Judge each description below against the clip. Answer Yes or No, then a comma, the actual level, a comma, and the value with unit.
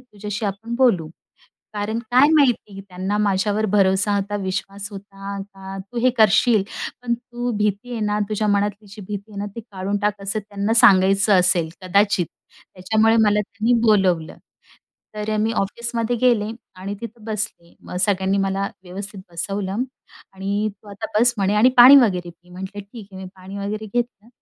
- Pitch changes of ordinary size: No, narrow, 2.1 semitones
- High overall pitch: Yes, high, 205 Hz